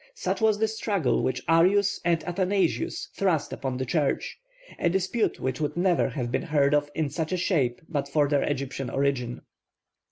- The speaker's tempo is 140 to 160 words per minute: No, average, 180 wpm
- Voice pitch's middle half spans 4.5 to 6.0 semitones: Yes, average, 5.0 semitones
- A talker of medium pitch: Yes, medium, 155 Hz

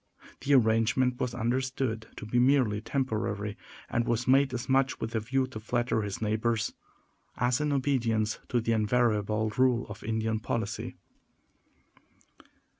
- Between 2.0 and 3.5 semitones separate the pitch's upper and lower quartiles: Yes, average, 2.8 semitones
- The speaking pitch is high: No, low, 115 Hz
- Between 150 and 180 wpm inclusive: No, average, 140 wpm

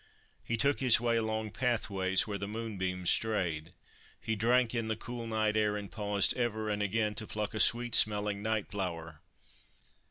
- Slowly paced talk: No, average, 170 wpm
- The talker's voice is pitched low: Yes, low, 110 Hz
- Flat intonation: Yes, narrow, 2.1 semitones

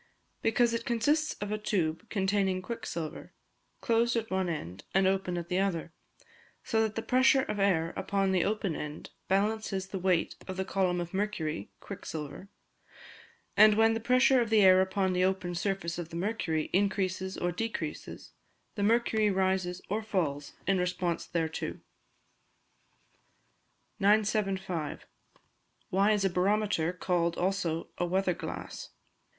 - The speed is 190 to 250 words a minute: No, average, 145 wpm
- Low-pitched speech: No, high, 190 Hz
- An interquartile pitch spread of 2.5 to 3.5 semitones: Yes, average, 3.2 semitones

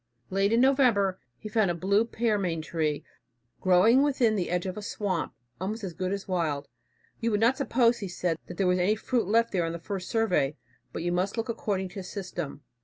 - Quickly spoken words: Yes, fast, 210 wpm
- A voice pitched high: Yes, high, 195 Hz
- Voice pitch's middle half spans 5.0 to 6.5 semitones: No, average, 4.0 semitones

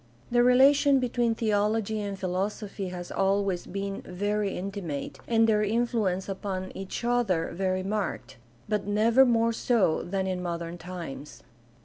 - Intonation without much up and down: No, average, 3.4 semitones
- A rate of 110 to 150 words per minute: Yes, slow, 135 wpm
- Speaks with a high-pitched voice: Yes, high, 200 Hz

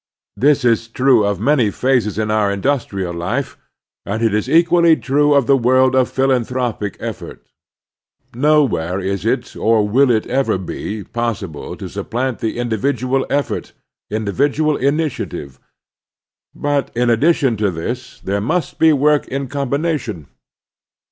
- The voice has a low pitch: Yes, low, 125 Hz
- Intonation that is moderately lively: Yes, average, 4.7 semitones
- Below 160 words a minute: Yes, slow, 135 wpm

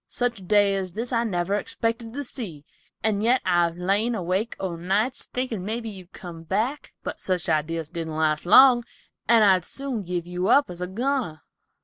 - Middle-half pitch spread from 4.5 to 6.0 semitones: Yes, average, 5.0 semitones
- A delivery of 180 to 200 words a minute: Yes, average, 195 wpm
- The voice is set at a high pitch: Yes, high, 195 Hz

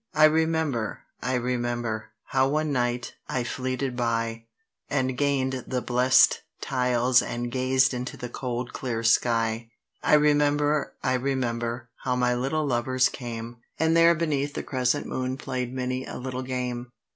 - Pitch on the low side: Yes, low, 125 Hz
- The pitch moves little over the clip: Yes, narrow, 2.0 semitones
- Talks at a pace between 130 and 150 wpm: Yes, average, 145 wpm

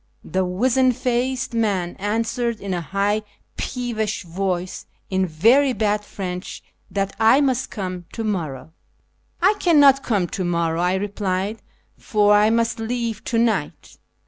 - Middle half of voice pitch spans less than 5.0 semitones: Yes, average, 4.2 semitones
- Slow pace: No, average, 145 wpm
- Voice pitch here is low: No, high, 210 Hz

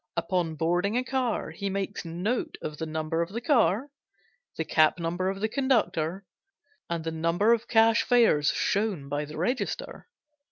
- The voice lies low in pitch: No, medium, 185 Hz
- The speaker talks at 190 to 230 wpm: No, average, 165 wpm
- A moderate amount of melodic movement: No, wide, 5.7 semitones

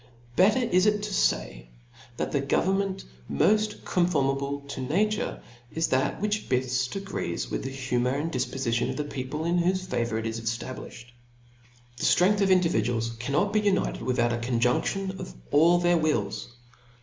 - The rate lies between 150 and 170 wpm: Yes, average, 160 wpm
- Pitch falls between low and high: Yes, medium, 145 Hz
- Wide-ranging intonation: Yes, wide, 7.4 semitones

